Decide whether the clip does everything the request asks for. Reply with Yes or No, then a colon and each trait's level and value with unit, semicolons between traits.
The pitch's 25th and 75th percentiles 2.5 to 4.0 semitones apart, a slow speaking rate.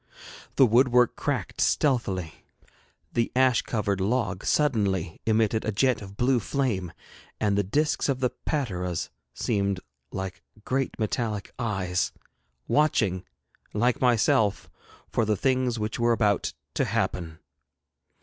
No: average, 4.4 semitones; slow, 120 wpm